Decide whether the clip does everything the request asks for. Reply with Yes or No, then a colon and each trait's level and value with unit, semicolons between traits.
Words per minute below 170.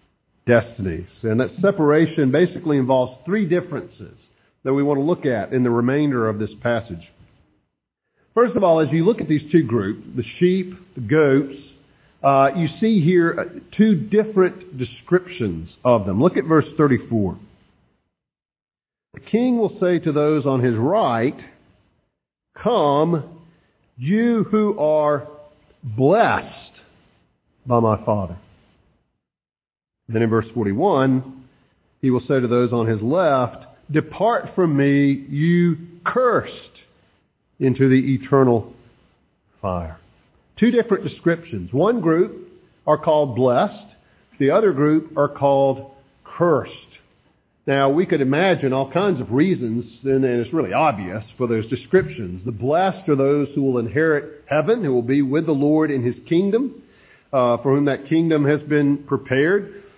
Yes: average, 140 wpm